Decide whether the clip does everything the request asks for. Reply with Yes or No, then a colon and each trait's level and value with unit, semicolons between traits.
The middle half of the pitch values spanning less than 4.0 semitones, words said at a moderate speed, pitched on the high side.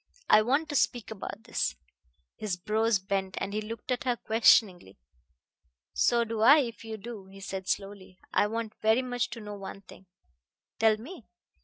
Yes: average, 2.9 semitones; average, 175 wpm; high, 215 Hz